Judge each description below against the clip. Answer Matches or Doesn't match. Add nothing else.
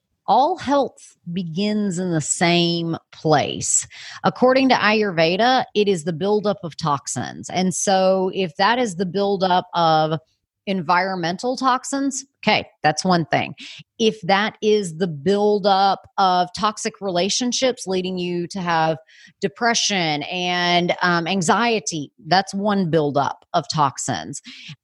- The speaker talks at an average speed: Doesn't match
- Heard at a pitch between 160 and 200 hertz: Matches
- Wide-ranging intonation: Doesn't match